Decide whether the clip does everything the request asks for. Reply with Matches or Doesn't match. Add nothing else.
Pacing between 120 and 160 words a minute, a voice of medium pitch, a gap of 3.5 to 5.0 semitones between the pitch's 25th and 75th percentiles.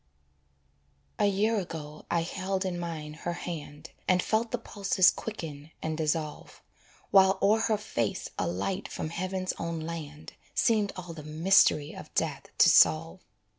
Matches